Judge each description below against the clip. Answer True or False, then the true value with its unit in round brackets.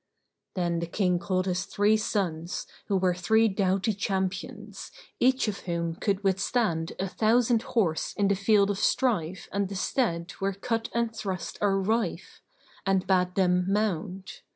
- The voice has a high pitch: True (195 Hz)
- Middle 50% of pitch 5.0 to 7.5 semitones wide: False (2.7 semitones)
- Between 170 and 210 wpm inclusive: False (155 wpm)